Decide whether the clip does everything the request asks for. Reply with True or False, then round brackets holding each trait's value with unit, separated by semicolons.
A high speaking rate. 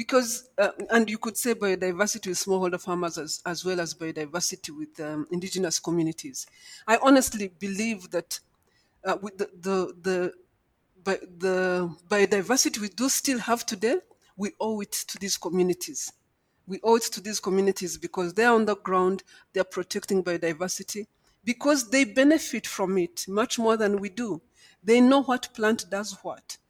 False (165 wpm)